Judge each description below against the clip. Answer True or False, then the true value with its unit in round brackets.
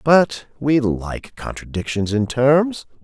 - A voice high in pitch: False (130 Hz)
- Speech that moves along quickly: False (120 wpm)